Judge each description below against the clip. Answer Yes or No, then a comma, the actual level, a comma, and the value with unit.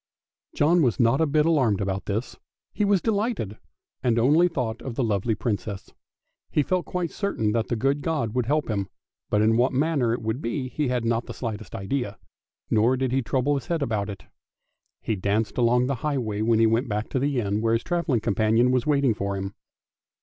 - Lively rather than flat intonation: No, average, 4.5 semitones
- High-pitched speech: No, low, 120 Hz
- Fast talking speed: Yes, fast, 210 wpm